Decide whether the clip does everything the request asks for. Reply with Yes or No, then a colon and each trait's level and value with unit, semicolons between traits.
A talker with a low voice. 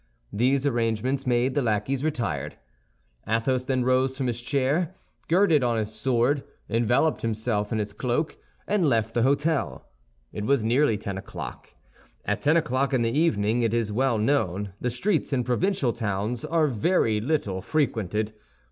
Yes: low, 125 Hz